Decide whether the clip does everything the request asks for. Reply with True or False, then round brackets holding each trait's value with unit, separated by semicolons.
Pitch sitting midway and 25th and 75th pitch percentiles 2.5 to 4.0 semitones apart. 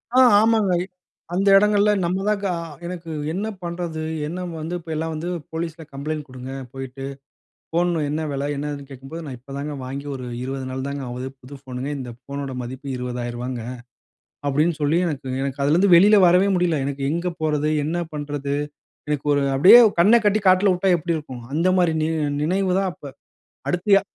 False (155 Hz; 4.4 semitones)